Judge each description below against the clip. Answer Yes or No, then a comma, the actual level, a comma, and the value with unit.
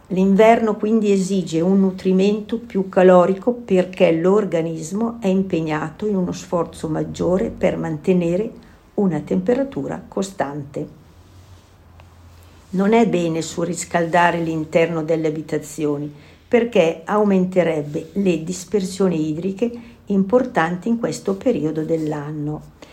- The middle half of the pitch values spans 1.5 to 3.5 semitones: No, average, 4.0 semitones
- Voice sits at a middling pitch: Yes, medium, 180 Hz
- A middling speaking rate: No, slow, 95 wpm